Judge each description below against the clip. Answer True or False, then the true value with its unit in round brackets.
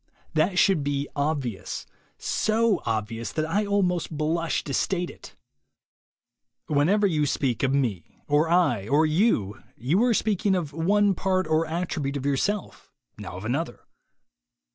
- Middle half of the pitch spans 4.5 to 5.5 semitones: True (5.1 semitones)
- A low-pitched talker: False (160 Hz)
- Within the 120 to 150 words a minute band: True (145 wpm)